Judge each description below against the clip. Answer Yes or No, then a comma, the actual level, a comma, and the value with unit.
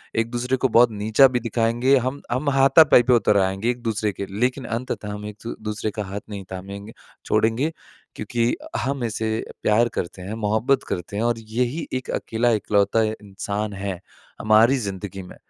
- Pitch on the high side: No, low, 110 Hz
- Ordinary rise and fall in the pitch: Yes, average, 3.1 semitones